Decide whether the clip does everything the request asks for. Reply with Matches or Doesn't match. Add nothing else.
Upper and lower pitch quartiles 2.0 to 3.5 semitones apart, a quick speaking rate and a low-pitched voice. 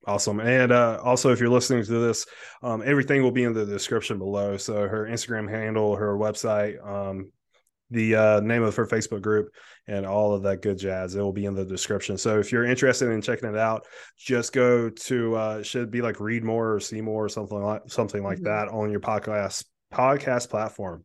Matches